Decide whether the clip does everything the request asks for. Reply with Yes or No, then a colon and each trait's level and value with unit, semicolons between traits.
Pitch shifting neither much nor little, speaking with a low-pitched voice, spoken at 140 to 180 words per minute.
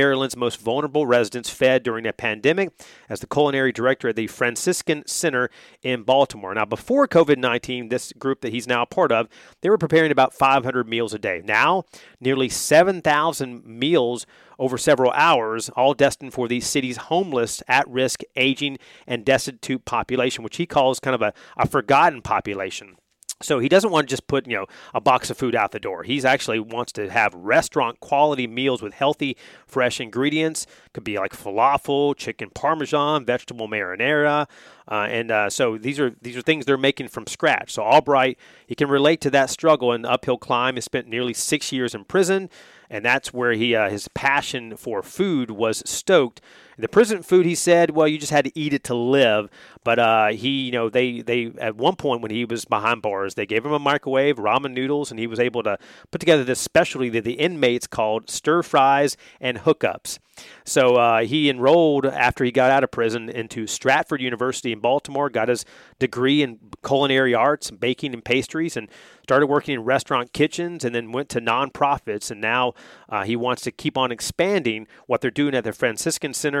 No: average, 3.2 semitones; low, 130 Hz; average, 195 wpm